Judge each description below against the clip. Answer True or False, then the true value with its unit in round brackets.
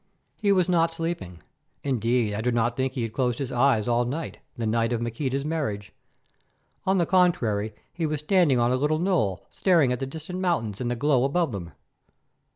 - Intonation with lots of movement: True (6.0 semitones)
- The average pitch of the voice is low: True (130 Hz)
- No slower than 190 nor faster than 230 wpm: True (195 wpm)